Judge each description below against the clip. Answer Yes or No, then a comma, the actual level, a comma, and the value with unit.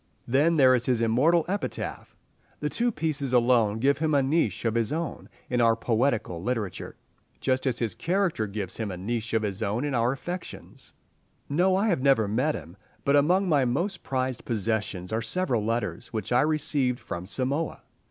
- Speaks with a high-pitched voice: No, low, 125 Hz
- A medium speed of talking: Yes, average, 180 wpm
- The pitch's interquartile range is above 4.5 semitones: Yes, average, 5.1 semitones